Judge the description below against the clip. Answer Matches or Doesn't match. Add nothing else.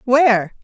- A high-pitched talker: Matches